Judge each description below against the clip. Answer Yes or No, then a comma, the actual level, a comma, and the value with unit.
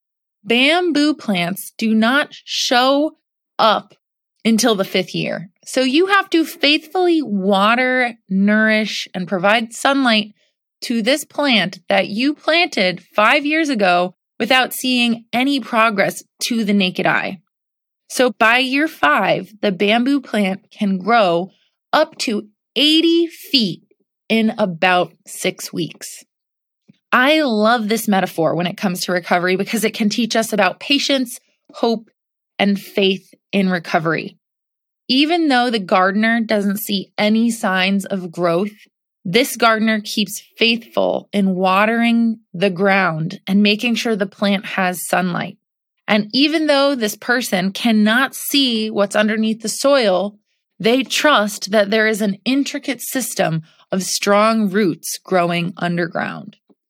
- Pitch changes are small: No, average, 4.5 semitones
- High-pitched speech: Yes, high, 215 Hz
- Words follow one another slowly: Yes, slow, 130 wpm